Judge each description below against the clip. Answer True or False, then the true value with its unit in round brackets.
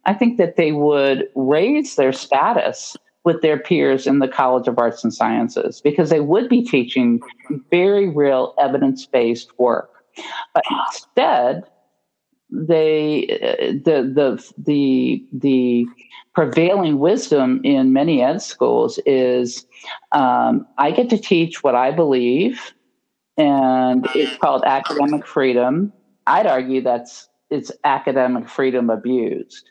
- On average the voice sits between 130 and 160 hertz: True (140 Hz)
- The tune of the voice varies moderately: False (6.8 semitones)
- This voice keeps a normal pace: False (125 wpm)